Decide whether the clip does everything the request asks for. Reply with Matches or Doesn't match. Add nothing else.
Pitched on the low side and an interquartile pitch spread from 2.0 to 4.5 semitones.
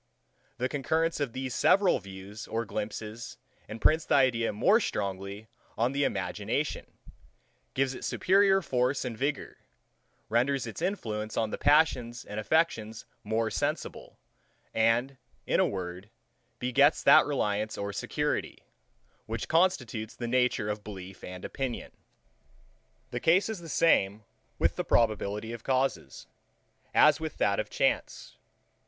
Doesn't match